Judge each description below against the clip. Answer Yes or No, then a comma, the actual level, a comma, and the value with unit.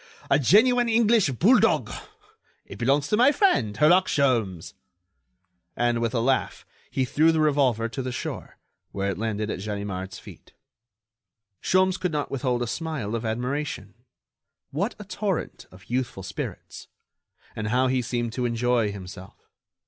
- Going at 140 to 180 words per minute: Yes, average, 150 wpm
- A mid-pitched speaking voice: No, low, 125 Hz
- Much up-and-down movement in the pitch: Yes, wide, 6.2 semitones